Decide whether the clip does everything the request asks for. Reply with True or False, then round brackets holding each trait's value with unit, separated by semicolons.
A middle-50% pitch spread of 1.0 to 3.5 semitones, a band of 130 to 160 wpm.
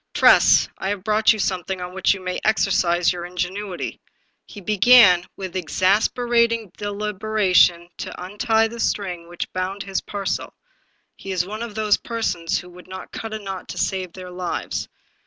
False (2.8 semitones; 175 wpm)